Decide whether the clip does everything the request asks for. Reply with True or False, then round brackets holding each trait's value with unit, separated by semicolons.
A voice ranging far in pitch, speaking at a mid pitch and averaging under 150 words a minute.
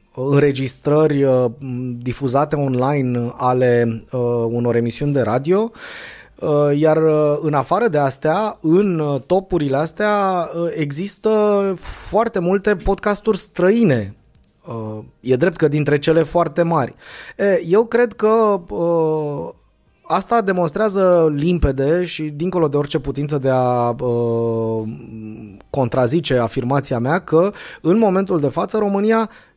True (6.5 semitones; 155 Hz; 120 wpm)